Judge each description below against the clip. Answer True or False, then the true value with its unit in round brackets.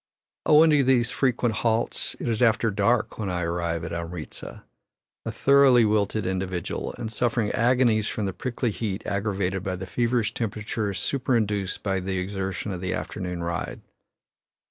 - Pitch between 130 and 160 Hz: False (105 Hz)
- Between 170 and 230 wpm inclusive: False (155 wpm)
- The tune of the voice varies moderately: True (4.0 semitones)